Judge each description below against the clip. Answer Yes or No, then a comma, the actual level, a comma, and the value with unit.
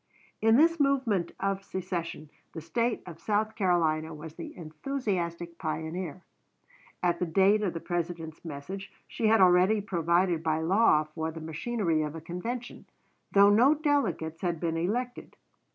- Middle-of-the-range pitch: Yes, medium, 175 Hz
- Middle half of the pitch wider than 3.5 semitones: Yes, average, 4.7 semitones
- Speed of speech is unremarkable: Yes, average, 150 wpm